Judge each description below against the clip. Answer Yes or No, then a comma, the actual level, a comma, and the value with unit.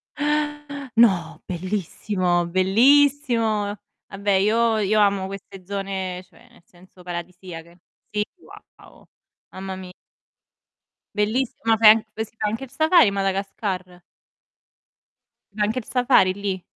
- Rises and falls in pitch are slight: No, average, 3.6 semitones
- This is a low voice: No, high, 200 Hz